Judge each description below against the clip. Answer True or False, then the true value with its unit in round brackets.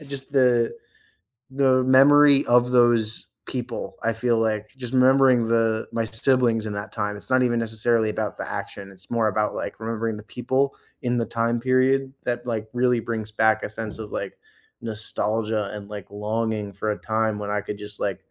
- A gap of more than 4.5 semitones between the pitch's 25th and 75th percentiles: False (2.6 semitones)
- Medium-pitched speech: False (115 Hz)